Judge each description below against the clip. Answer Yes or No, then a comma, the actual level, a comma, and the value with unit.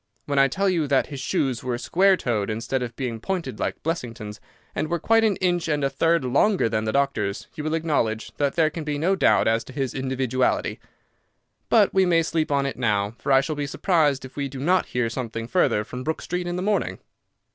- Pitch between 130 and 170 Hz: Yes, medium, 140 Hz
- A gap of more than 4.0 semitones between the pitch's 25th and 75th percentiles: Yes, average, 5.1 semitones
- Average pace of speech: No, fast, 225 wpm